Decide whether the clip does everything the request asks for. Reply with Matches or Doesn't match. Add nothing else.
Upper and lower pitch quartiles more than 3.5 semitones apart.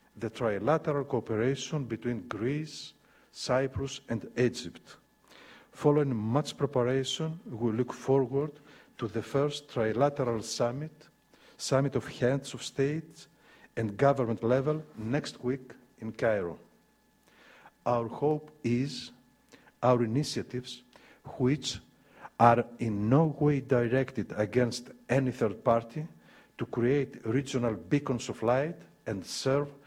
Doesn't match